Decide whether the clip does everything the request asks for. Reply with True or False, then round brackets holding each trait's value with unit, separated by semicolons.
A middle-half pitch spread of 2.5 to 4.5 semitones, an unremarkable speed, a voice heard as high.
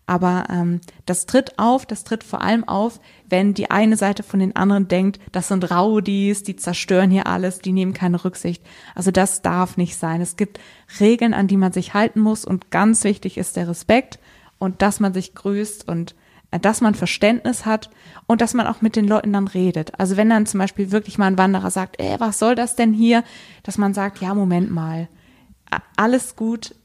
False (2.8 semitones; 205 wpm; 200 Hz)